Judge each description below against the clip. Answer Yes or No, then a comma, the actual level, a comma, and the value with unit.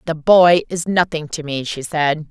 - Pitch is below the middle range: No, medium, 160 Hz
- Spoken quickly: Yes, fast, 210 wpm